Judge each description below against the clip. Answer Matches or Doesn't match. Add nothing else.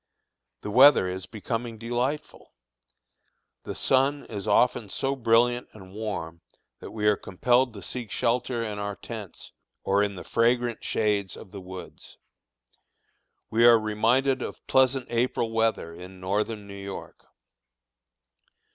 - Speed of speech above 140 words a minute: Doesn't match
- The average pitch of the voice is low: Matches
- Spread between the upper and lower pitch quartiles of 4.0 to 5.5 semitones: Doesn't match